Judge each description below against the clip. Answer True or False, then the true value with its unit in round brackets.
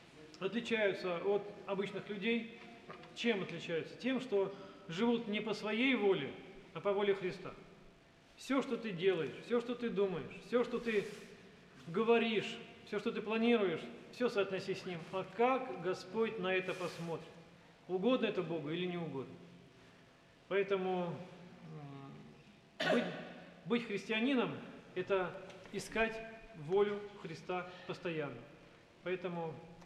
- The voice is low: False (195 Hz)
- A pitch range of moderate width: True (4.1 semitones)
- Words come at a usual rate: True (120 wpm)